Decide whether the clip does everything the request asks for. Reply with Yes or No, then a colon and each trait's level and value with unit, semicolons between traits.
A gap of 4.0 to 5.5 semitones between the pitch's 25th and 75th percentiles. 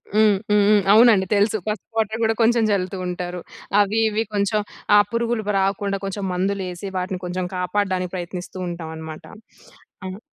No: average, 2.8 semitones